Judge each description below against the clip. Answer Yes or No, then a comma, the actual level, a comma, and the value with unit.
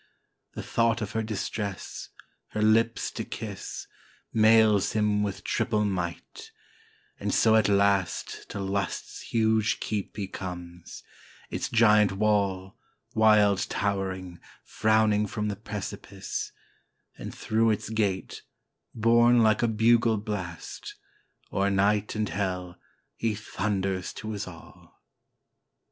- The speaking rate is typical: No, slow, 120 wpm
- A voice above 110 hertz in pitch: No, low, 105 Hz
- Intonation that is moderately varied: No, narrow, 2.1 semitones